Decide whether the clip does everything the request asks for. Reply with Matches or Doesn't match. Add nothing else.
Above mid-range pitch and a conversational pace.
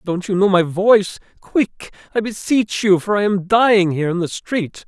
Doesn't match